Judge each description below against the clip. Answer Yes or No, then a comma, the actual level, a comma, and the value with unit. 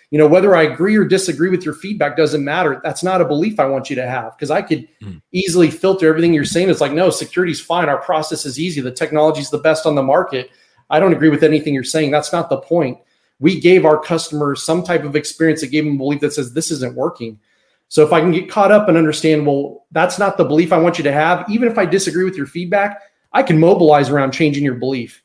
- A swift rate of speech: Yes, fast, 255 wpm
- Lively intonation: No, average, 3.1 semitones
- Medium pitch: Yes, medium, 160 Hz